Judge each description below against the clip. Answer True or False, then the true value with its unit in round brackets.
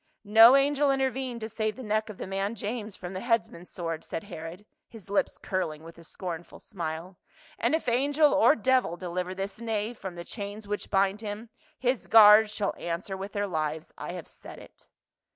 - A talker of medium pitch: False (205 Hz)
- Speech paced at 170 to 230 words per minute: True (200 wpm)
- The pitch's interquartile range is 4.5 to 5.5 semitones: False (4.1 semitones)